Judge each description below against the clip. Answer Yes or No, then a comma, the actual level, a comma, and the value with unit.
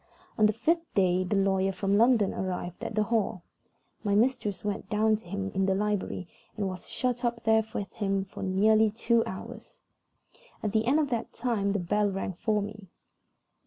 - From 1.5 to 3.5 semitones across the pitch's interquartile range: Yes, narrow, 2.5 semitones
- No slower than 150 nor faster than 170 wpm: No, average, 190 wpm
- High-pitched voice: Yes, high, 205 Hz